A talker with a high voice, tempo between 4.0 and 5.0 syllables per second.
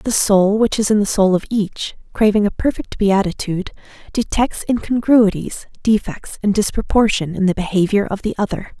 No: high, 205 Hz; 5.2 syllables/s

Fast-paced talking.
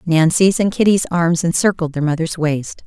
No: average, 170 wpm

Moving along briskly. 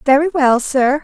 No: average, 175 wpm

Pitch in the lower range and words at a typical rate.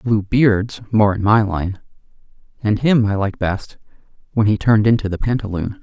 Yes: low, 105 Hz; average, 175 wpm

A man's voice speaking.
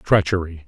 Yes: male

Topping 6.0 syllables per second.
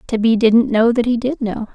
No: 5.1 syllables/s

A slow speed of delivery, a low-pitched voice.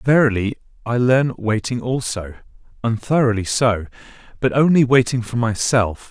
Yes: slow, 120 wpm; low, 120 Hz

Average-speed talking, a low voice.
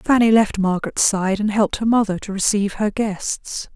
No: average, 190 wpm; high, 205 Hz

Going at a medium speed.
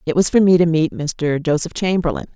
No: fast, 230 wpm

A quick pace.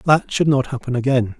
Yes: fast, 215 wpm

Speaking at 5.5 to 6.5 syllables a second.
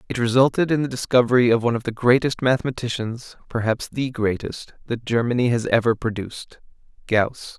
Yes: 5.7 syllables/s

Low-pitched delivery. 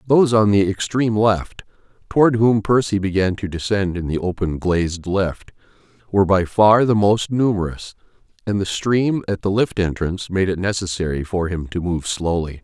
Yes: low, 100 Hz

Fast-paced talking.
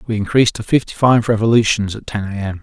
Yes: fast, 230 wpm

